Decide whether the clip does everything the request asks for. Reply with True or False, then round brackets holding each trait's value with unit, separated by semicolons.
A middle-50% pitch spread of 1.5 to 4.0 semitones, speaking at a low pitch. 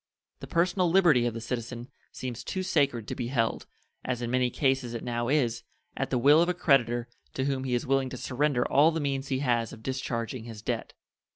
True (2.9 semitones; 130 Hz)